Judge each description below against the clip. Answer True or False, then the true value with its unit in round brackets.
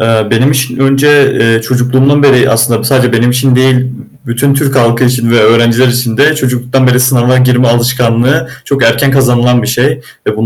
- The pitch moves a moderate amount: False (2.1 semitones)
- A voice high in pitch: False (125 Hz)